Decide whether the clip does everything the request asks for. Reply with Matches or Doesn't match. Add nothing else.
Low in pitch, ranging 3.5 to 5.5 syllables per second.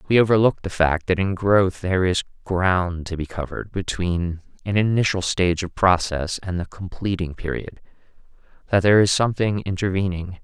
Matches